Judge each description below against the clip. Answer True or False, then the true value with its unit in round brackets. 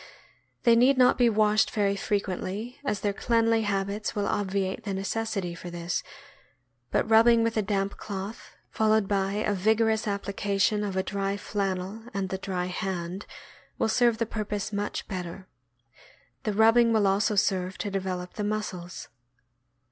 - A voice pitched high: True (205 Hz)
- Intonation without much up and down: True (2.3 semitones)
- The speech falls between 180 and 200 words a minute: False (155 wpm)